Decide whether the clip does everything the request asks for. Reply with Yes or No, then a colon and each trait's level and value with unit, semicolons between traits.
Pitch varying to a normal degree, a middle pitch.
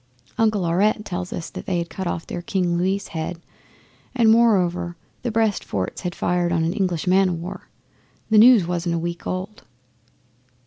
Yes: average, 3.1 semitones; medium, 180 Hz